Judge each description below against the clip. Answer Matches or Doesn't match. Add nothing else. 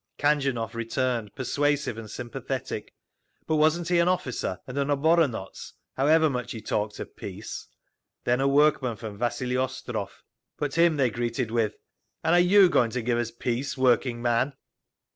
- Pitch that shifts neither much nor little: Matches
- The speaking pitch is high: Doesn't match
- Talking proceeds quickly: Doesn't match